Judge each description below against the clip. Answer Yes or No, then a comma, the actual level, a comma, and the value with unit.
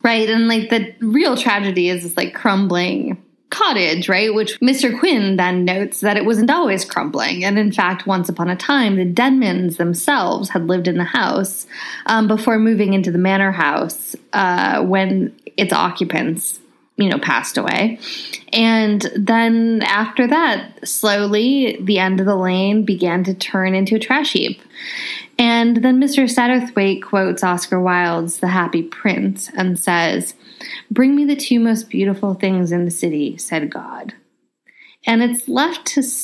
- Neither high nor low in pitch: No, high, 205 Hz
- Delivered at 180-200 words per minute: No, average, 160 wpm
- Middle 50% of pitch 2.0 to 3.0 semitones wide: No, average, 4.3 semitones